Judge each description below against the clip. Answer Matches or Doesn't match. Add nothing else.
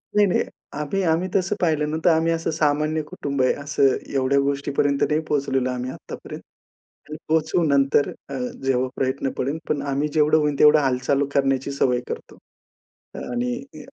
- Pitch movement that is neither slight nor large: Doesn't match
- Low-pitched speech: Doesn't match